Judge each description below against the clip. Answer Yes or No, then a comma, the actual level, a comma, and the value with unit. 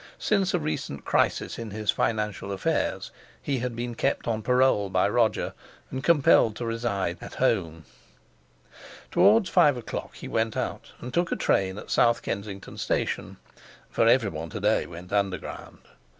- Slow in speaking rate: No, average, 150 wpm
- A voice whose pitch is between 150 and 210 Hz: No, low, 115 Hz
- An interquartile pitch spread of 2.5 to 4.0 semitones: No, average, 4.8 semitones